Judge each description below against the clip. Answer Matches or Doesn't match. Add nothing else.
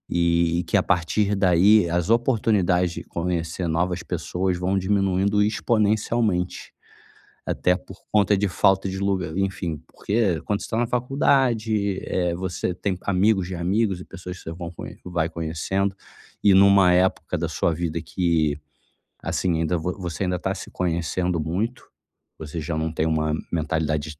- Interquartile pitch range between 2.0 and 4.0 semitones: Matches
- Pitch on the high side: Doesn't match